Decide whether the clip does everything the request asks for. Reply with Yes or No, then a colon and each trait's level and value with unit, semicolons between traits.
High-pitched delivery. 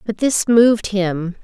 Yes: high, 205 Hz